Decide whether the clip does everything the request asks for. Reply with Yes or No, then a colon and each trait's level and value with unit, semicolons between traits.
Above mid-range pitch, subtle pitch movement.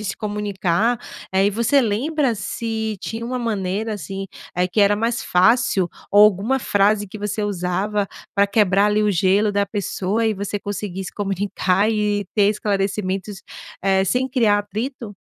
Yes: high, 205 Hz; narrow, 2.1 semitones